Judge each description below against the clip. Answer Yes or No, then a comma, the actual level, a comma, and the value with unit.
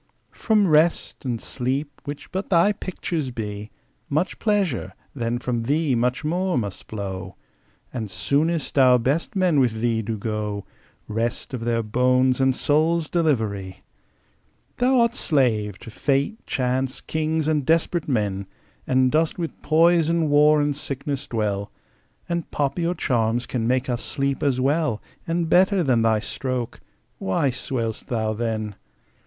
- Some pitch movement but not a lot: No, wide, 5.7 semitones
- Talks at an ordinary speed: Yes, average, 145 wpm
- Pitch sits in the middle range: No, low, 130 Hz